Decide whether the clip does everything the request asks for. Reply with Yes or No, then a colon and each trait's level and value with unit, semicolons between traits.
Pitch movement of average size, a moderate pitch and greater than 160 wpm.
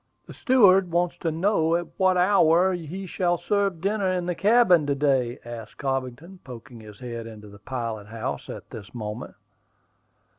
No: wide, 7.6 semitones; medium, 160 Hz; average, 170 wpm